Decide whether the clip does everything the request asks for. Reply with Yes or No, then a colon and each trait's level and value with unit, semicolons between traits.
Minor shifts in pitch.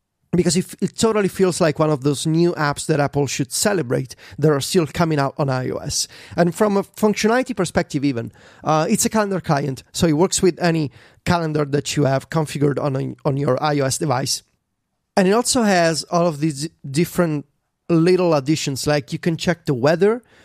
No: average, 3.7 semitones